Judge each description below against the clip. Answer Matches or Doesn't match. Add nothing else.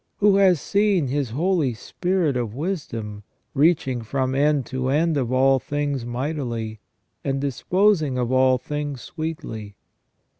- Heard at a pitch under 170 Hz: Matches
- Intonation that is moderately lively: Matches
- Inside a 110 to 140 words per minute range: Matches